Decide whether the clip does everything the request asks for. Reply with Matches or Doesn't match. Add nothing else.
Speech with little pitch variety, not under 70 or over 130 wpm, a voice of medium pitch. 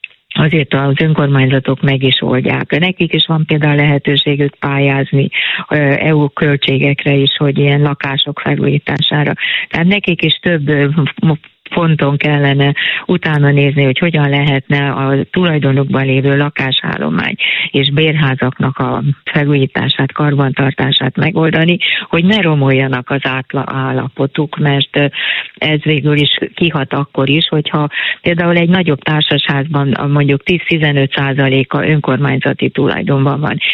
Matches